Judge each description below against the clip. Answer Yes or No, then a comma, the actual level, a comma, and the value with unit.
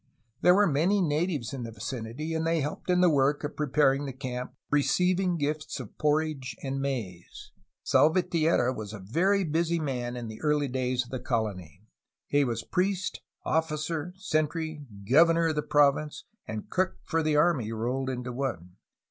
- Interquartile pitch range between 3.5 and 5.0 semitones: Yes, average, 4.6 semitones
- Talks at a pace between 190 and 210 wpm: No, average, 165 wpm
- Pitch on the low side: No, medium, 145 Hz